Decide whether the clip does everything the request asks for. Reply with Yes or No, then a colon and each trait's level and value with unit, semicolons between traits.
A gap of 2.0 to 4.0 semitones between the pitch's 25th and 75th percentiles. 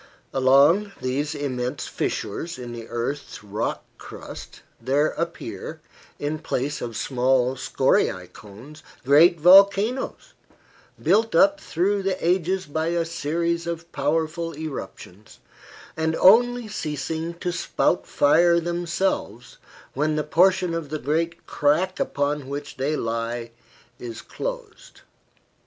No: average, 4.4 semitones